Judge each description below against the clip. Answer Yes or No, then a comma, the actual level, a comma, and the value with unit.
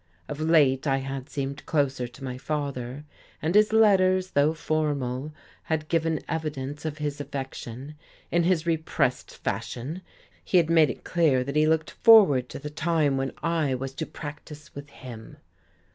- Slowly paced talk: No, average, 160 wpm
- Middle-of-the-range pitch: Yes, medium, 150 Hz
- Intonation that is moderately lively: Yes, average, 3.1 semitones